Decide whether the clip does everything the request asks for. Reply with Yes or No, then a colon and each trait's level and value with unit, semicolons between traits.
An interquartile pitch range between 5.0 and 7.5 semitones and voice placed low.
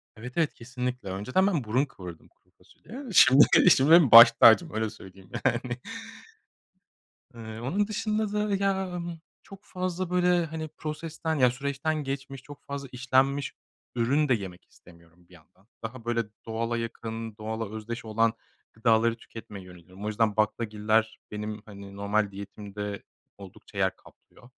Yes: wide, 5.6 semitones; low, 115 Hz